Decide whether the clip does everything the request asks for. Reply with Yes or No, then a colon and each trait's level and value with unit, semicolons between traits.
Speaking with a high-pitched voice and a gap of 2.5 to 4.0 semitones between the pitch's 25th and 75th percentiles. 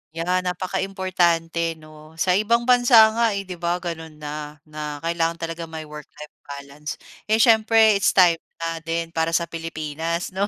No: medium, 165 Hz; average, 3.2 semitones